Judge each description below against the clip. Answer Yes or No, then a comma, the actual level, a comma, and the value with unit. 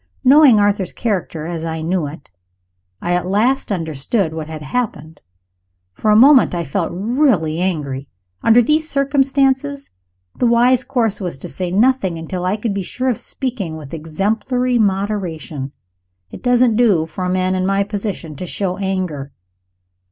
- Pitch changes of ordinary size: No, wide, 6.8 semitones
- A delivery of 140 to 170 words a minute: Yes, average, 160 wpm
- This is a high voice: Yes, high, 195 Hz